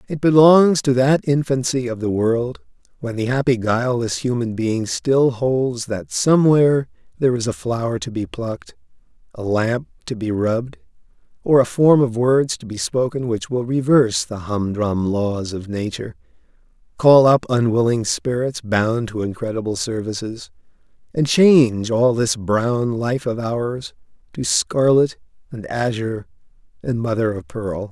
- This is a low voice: Yes, low, 120 Hz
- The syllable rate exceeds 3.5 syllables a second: Yes, 4.5 syllables/s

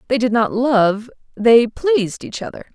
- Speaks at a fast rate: No, average, 175 wpm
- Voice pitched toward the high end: Yes, high, 235 Hz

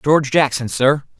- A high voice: No, medium, 140 Hz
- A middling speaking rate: Yes, average, 150 wpm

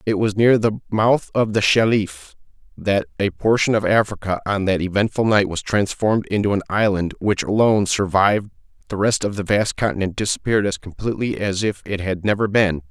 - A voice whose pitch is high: No, low, 100 Hz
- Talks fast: No, average, 185 wpm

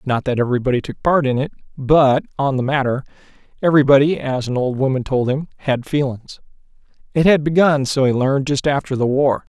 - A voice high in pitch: No, low, 135 Hz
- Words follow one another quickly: No, average, 190 wpm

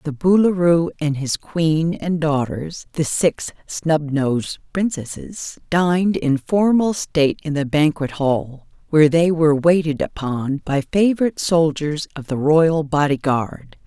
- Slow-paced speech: Yes, slow, 125 wpm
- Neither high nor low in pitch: Yes, medium, 155 Hz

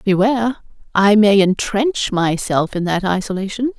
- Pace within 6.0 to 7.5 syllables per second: No, 4.6 syllables/s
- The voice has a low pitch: No, high, 205 Hz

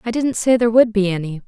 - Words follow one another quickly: Yes, fast, 285 wpm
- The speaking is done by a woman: Yes, female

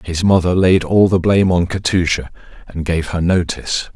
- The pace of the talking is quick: No, average, 180 wpm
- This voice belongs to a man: Yes, male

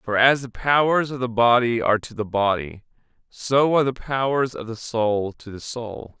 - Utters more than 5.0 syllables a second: No, 4.8 syllables/s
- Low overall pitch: Yes, low, 120 Hz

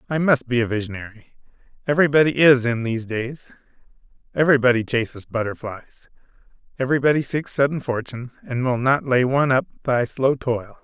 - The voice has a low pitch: Yes, low, 125 Hz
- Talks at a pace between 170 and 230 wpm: No, average, 145 wpm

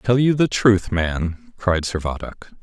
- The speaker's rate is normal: Yes, average, 160 wpm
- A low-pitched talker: Yes, low, 100 Hz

